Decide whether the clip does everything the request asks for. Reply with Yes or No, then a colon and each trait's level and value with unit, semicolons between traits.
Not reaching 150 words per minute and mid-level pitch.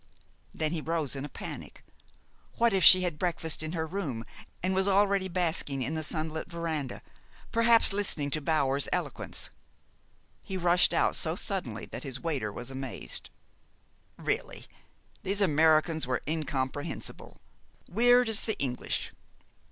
Yes: average, 140 wpm; medium, 160 Hz